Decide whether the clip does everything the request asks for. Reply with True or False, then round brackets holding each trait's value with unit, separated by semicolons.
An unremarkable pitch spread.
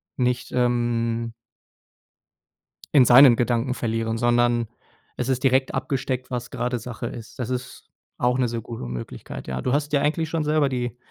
False (1.8 semitones)